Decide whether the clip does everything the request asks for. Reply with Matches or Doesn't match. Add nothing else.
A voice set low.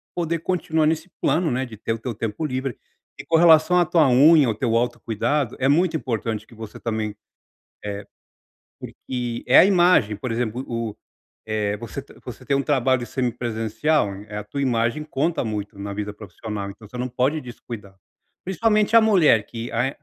Matches